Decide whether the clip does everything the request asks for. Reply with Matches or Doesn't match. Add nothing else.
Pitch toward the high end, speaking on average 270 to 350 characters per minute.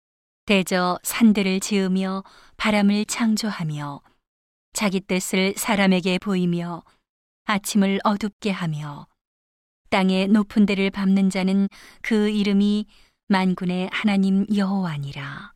Doesn't match